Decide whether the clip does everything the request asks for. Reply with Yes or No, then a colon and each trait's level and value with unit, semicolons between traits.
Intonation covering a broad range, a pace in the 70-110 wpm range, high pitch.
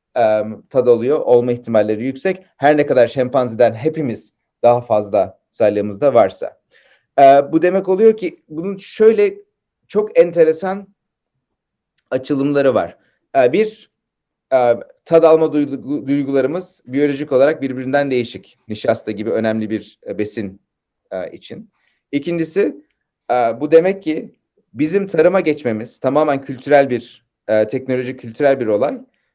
No: wide, 6.7 semitones; average, 105 wpm; medium, 140 Hz